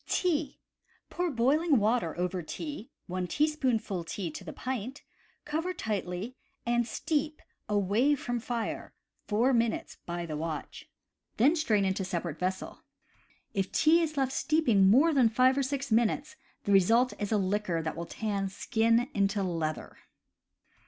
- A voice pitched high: Yes, high, 225 Hz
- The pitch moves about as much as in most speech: No, wide, 6.2 semitones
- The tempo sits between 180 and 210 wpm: No, average, 150 wpm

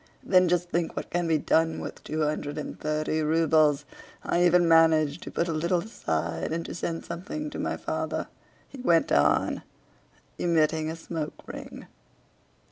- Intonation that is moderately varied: No, narrow, 2.0 semitones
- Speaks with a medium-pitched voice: Yes, medium, 165 Hz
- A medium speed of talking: Yes, average, 165 wpm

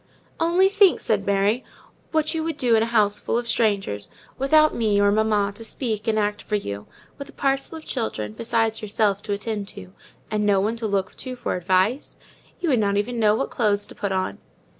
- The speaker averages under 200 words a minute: No, fast, 205 wpm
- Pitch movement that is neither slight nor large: Yes, average, 3.4 semitones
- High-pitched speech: Yes, high, 215 Hz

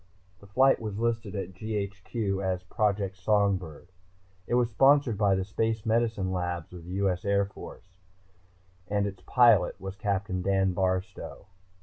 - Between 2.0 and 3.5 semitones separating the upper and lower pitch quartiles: Yes, narrow, 2.6 semitones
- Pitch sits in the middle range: No, low, 100 Hz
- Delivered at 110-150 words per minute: Yes, average, 145 wpm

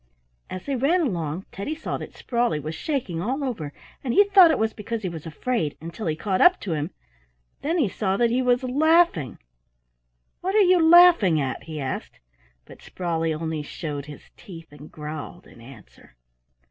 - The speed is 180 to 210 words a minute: Yes, average, 185 wpm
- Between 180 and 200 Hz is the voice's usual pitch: Yes, high, 190 Hz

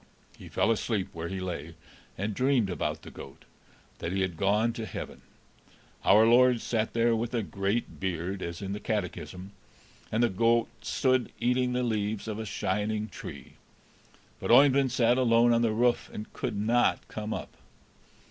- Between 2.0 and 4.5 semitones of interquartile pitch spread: Yes, average, 3.4 semitones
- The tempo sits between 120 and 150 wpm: No, average, 170 wpm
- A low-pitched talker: Yes, low, 110 Hz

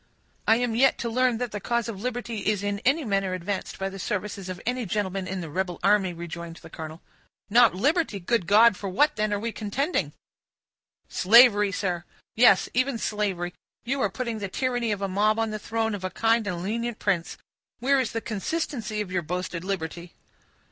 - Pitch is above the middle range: Yes, high, 210 Hz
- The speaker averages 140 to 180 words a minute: No, average, 195 wpm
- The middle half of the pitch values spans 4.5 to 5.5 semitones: No, average, 3.9 semitones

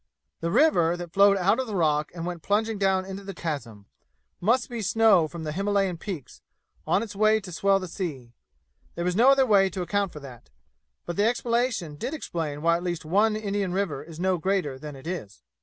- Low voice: No, medium, 185 Hz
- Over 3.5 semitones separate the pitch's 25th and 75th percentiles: Yes, average, 3.9 semitones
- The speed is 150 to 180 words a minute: No, fast, 205 wpm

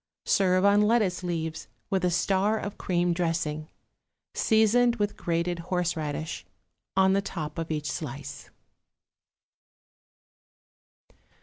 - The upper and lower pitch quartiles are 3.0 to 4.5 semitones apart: Yes, average, 3.5 semitones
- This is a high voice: No, medium, 180 Hz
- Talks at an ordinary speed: No, slow, 105 wpm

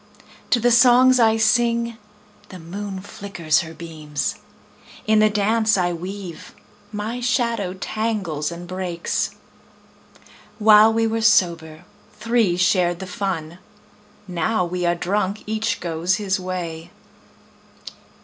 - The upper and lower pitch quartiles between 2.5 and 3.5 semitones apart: No, average, 4.3 semitones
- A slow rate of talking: Yes, slow, 120 wpm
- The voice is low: No, high, 195 Hz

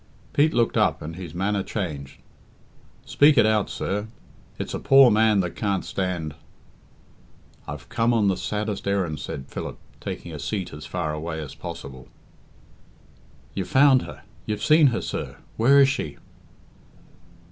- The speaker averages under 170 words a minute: Yes, average, 155 wpm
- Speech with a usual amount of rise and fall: No, wide, 6.0 semitones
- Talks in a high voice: No, low, 100 Hz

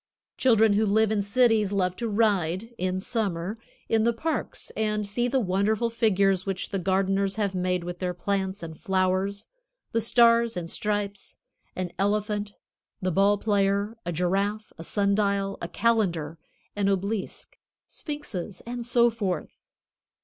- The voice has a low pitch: No, high, 200 Hz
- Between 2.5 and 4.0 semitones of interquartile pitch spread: Yes, average, 2.8 semitones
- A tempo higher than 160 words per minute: No, average, 150 wpm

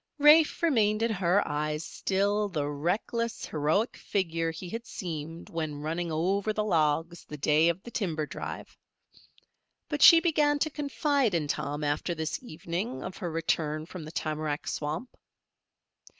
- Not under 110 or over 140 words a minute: No, average, 150 wpm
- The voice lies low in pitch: No, medium, 170 Hz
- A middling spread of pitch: No, wide, 6.0 semitones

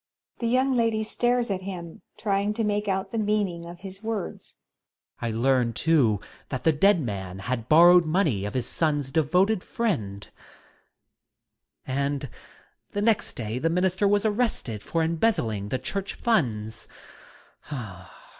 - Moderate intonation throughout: No, wide, 8.3 semitones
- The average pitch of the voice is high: No, medium, 170 Hz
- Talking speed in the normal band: Yes, average, 150 wpm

